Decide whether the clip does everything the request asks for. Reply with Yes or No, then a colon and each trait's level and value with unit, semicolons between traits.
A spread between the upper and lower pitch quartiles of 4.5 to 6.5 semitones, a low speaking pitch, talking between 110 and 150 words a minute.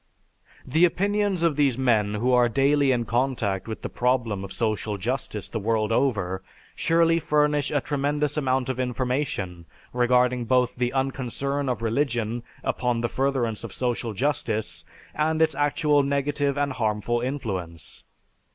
No: average, 3.9 semitones; low, 125 Hz; average, 145 wpm